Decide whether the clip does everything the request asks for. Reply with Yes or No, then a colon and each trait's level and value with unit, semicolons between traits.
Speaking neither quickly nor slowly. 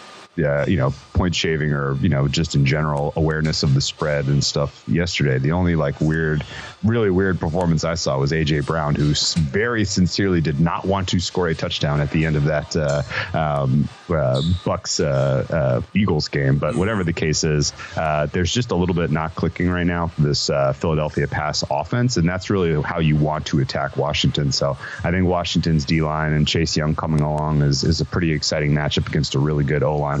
No: fast, 210 wpm